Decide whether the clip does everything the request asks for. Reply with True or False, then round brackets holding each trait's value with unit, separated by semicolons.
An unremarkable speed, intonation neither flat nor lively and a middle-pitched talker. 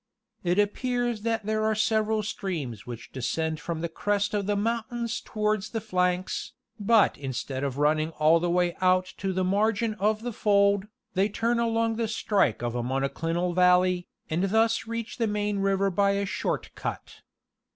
False (170 wpm; 4.0 semitones; 200 Hz)